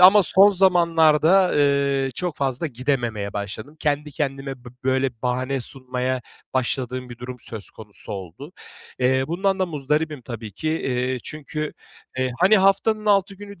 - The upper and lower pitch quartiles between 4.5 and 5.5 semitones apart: Yes, average, 5.1 semitones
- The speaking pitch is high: No, medium, 140 Hz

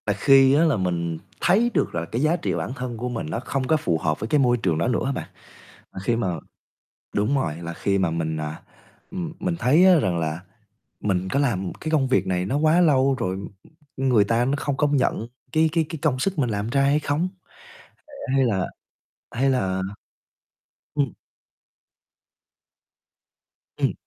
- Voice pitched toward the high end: No, low, 125 Hz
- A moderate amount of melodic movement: No, wide, 7.6 semitones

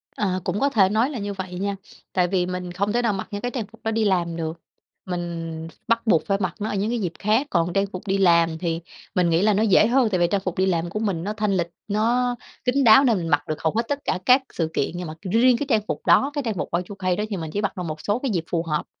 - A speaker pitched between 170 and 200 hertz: Yes, high, 195 Hz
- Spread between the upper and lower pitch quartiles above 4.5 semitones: No, average, 4.2 semitones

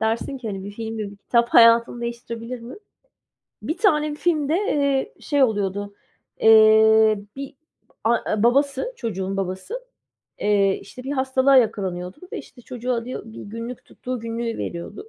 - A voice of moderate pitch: No, high, 230 Hz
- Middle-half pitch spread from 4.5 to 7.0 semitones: No, average, 3.7 semitones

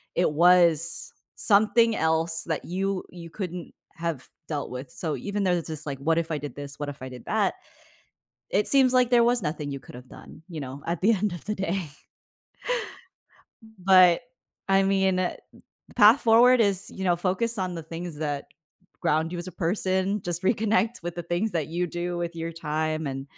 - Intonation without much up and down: No, average, 3.6 semitones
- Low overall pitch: No, medium, 175 Hz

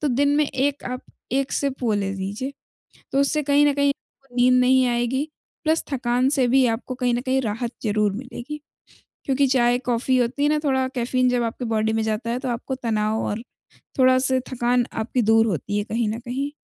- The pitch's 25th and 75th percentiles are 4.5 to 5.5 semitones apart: No, narrow, 2.6 semitones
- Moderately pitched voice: No, very high, 250 Hz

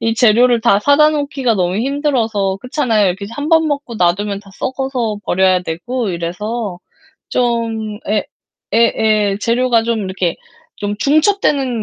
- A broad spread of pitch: No, average, 4.2 semitones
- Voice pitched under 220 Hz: No, high, 225 Hz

